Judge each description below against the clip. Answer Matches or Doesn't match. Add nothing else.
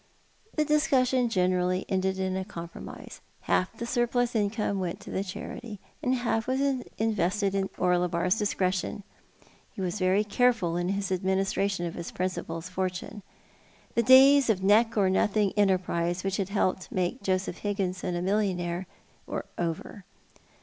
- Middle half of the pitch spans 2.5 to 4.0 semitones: Matches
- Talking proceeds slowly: Doesn't match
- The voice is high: Matches